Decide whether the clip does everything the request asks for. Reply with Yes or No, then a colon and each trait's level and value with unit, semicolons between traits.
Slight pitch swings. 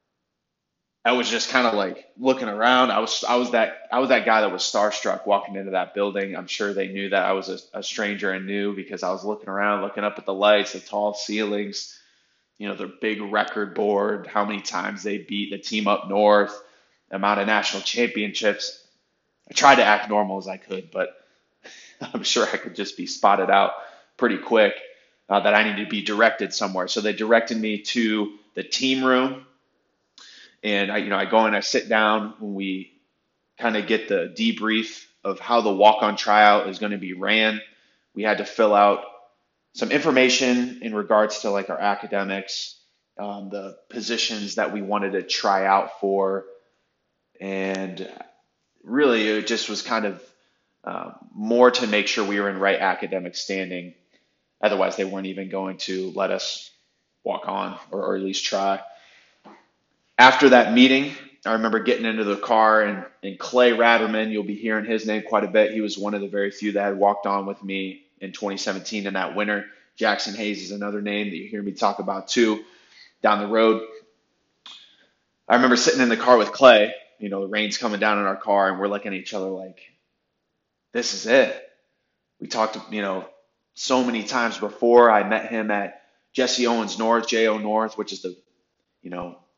Yes: narrow, 2.0 semitones